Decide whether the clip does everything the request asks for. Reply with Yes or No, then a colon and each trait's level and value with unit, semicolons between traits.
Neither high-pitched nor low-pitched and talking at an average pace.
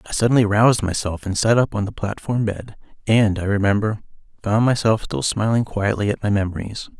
No: low, 105 Hz; average, 190 wpm